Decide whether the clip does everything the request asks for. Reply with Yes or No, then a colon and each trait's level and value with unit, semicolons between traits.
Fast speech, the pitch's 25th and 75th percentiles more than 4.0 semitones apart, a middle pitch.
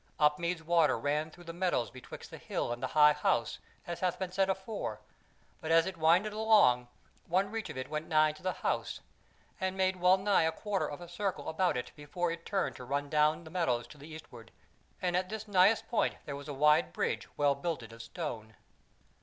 Yes: fast, 210 wpm; average, 4.4 semitones; medium, 165 Hz